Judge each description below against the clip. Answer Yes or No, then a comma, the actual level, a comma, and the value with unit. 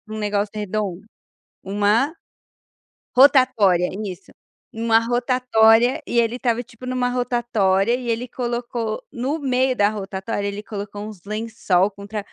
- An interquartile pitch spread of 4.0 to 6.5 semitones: No, average, 3.2 semitones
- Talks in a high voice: Yes, high, 225 Hz